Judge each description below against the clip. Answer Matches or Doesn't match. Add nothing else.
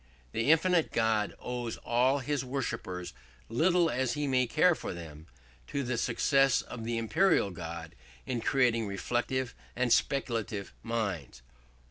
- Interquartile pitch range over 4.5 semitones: Doesn't match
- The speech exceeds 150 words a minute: Doesn't match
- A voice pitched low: Matches